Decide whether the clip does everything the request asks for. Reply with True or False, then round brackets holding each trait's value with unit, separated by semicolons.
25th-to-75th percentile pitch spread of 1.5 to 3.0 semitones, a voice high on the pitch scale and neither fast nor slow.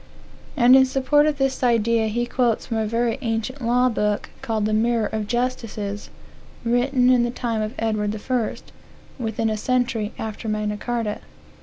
True (2.4 semitones; 230 Hz; 165 wpm)